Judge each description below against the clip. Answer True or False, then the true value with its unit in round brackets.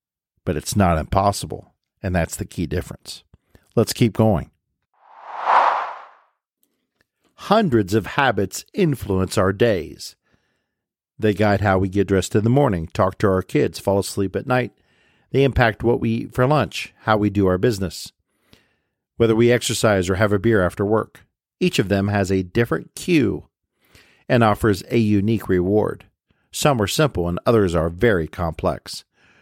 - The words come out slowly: False (155 wpm)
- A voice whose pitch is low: True (105 Hz)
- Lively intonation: False (3.7 semitones)